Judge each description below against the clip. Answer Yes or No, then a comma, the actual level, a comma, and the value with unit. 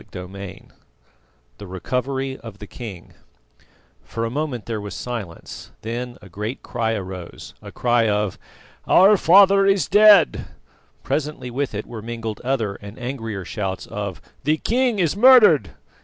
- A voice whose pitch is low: Yes, low, 120 Hz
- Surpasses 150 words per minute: No, average, 145 wpm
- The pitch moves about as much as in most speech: No, wide, 6.3 semitones